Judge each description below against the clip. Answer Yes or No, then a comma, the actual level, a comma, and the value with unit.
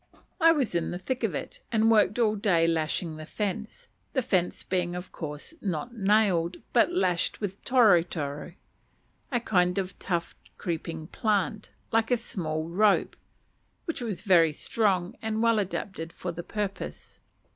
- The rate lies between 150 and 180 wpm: Yes, average, 155 wpm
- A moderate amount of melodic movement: Yes, average, 4.5 semitones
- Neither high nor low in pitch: No, high, 195 Hz